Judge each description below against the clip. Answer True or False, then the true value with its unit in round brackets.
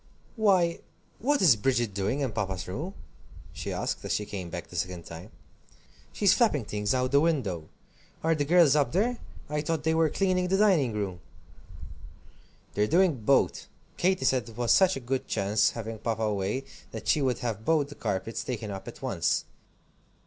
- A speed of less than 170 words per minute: False (185 wpm)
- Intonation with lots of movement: True (7.8 semitones)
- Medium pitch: False (130 Hz)